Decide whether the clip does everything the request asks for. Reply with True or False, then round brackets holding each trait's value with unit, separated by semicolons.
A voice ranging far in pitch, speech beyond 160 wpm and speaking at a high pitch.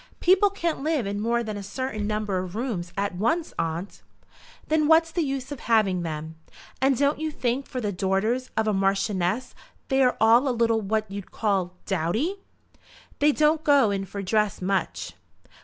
True (5.8 semitones; 175 wpm; 220 Hz)